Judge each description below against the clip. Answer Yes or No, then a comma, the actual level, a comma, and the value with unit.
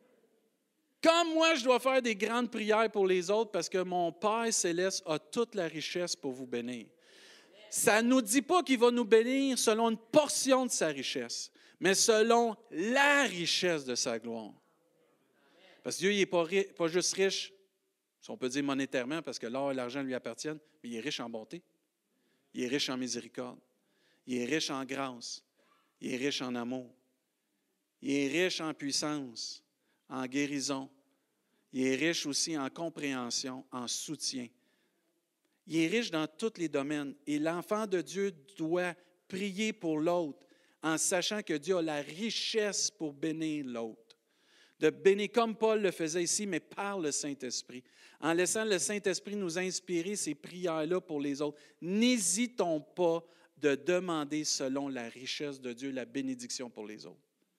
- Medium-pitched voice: Yes, medium, 170 Hz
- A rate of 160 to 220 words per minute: Yes, average, 170 wpm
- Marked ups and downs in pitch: Yes, wide, 7.1 semitones